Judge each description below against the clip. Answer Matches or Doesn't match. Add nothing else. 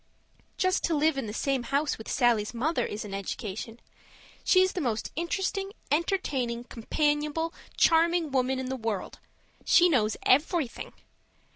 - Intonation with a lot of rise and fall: Matches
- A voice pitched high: Matches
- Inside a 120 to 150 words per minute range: Matches